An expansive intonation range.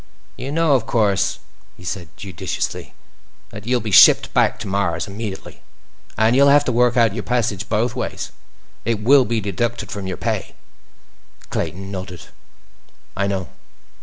No: average, 3.9 semitones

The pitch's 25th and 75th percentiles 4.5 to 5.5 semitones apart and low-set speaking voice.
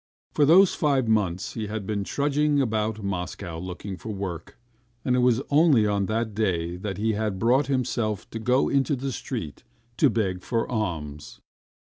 Yes: average, 4.8 semitones; low, 110 Hz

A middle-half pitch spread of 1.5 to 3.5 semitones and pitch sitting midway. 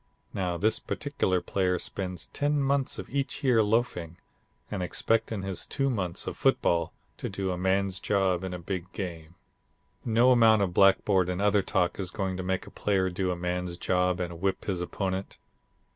No: narrow, 2.5 semitones; very low, 95 Hz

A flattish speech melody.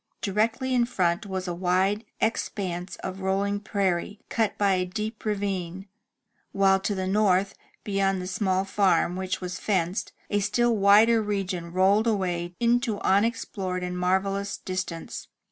Yes: narrow, 2.1 semitones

